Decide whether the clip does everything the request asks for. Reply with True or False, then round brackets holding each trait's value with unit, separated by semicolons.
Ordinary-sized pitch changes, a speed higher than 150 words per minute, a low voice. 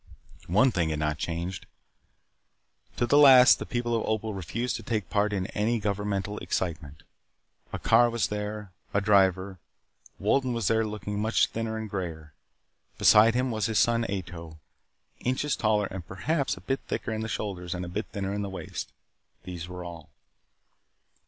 True (3.7 semitones; 170 wpm; 105 Hz)